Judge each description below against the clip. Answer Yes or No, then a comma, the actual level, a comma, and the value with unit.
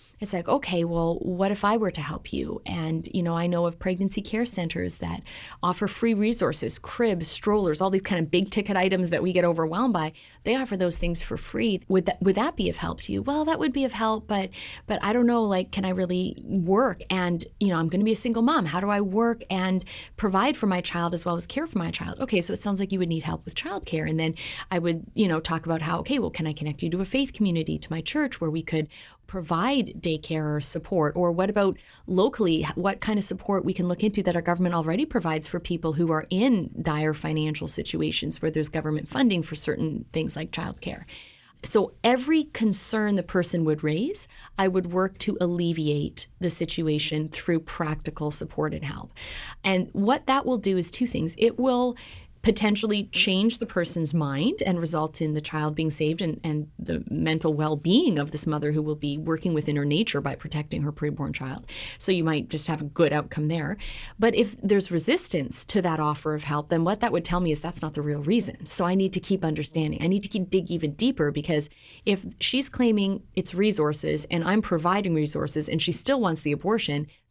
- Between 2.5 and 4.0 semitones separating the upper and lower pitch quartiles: No, average, 4.7 semitones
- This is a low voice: No, medium, 180 Hz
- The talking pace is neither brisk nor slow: No, fast, 225 wpm